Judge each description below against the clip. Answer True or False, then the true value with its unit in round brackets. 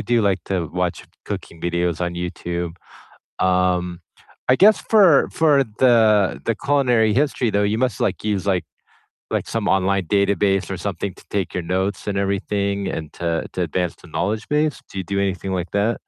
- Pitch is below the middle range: True (100 Hz)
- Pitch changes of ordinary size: True (3.4 semitones)